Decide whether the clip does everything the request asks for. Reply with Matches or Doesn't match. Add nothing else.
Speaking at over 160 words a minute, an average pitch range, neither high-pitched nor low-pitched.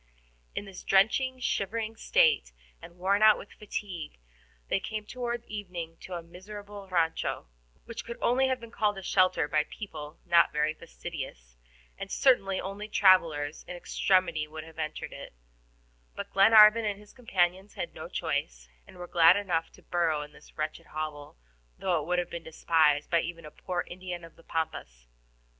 Matches